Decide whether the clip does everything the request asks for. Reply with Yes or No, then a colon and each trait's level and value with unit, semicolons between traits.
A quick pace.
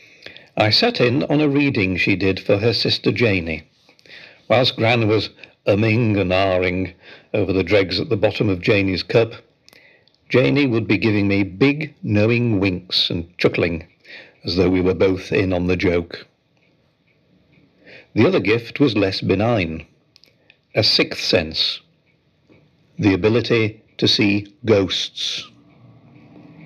No: slow, 135 wpm